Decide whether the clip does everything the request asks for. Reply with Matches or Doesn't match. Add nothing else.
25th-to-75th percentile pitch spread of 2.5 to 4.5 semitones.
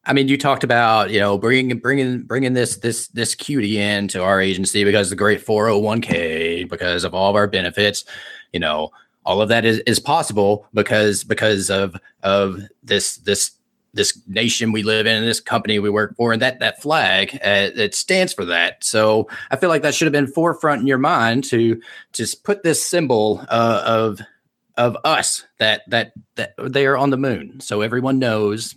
Matches